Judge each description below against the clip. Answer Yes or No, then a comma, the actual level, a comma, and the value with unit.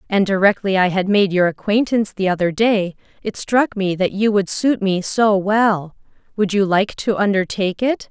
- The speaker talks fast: No, average, 190 wpm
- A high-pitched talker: Yes, high, 200 Hz